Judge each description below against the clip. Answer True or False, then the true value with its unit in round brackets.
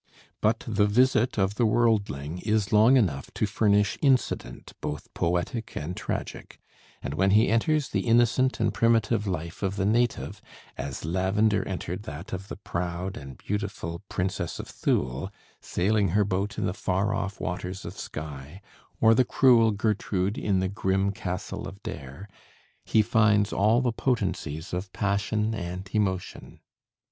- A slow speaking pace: False (155 wpm)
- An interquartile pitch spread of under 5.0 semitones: True (3.4 semitones)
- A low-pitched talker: True (100 Hz)